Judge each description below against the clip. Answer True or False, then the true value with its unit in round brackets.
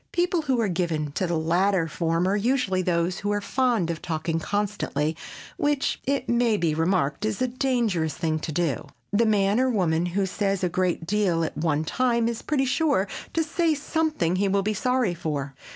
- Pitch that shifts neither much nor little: False (6.4 semitones)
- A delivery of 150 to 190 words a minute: True (185 wpm)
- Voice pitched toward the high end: True (195 Hz)